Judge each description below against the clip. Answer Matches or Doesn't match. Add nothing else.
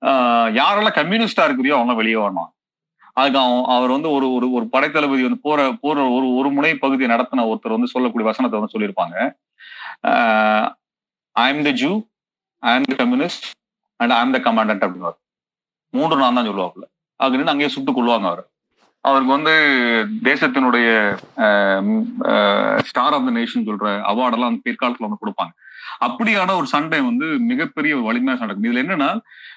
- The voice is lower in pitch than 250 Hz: Matches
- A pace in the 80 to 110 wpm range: Doesn't match